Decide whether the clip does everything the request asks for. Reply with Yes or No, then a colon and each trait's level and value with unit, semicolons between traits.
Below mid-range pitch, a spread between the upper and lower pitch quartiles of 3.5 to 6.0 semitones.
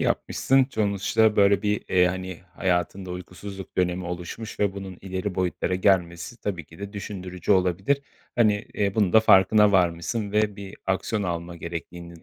No: very low, 95 Hz; narrow, 2.5 semitones